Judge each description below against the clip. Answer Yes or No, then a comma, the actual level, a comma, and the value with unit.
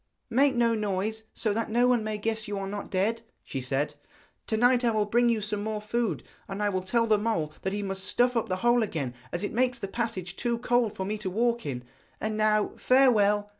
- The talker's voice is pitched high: Yes, high, 215 Hz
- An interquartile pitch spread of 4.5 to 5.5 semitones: No, average, 3.0 semitones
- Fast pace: Yes, fast, 235 wpm